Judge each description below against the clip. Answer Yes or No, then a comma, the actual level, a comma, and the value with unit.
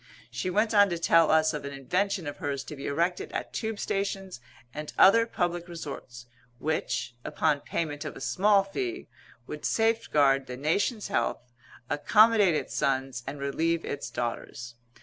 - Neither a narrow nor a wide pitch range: No, wide, 6.1 semitones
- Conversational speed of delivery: Yes, average, 160 wpm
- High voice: No, medium, 160 Hz